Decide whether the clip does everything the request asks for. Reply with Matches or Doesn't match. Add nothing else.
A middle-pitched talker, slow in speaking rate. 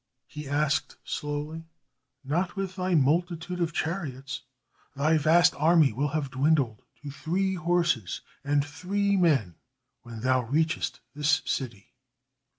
Matches